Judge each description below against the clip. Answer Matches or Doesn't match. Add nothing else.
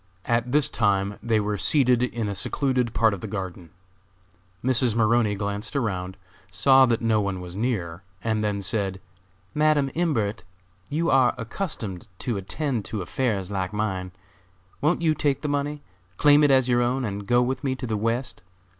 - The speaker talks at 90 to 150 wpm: Doesn't match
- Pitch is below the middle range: Matches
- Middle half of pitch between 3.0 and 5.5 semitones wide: Matches